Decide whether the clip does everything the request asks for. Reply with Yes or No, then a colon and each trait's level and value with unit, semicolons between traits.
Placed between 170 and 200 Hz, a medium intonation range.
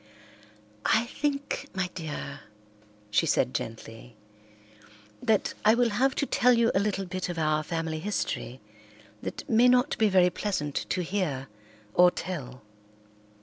No: medium, 185 Hz; wide, 6.5 semitones